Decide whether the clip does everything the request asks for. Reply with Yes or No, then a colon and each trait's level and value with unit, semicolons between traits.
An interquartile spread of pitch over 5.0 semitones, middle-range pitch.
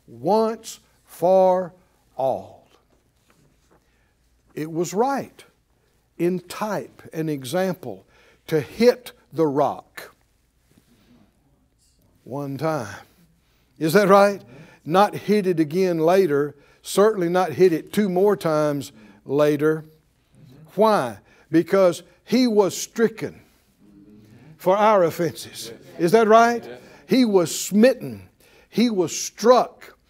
Yes: wide, 5.5 semitones; medium, 175 Hz